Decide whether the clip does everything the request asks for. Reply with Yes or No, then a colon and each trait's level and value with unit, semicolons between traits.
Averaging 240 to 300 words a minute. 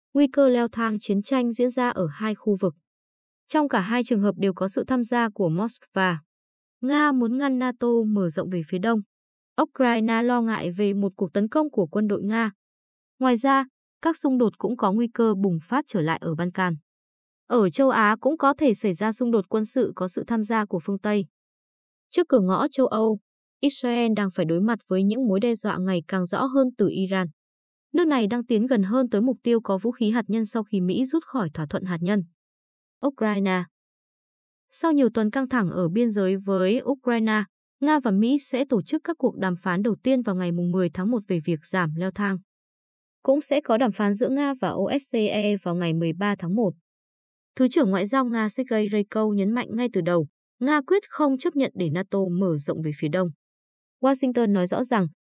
No: average, 215 wpm